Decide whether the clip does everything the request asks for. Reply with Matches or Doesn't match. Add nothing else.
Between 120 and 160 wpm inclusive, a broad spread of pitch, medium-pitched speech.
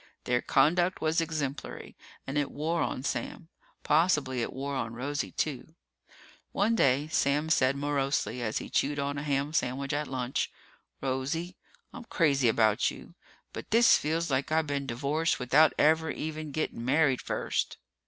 Doesn't match